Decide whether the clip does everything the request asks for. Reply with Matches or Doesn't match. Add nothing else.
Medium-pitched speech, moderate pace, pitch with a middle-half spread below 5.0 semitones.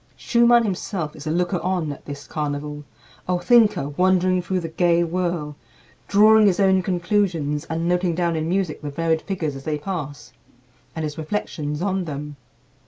Matches